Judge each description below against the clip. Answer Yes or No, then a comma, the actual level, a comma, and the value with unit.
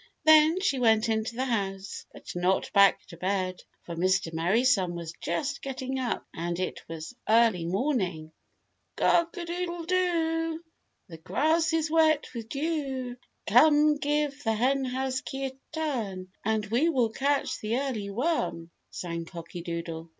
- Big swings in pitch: Yes, wide, 8.2 semitones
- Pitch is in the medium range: No, high, 240 Hz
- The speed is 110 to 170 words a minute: Yes, average, 150 wpm